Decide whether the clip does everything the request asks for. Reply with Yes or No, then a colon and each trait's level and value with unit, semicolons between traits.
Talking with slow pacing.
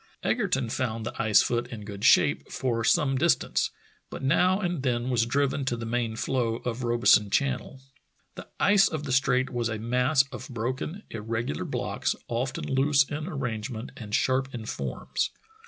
No: average, 170 wpm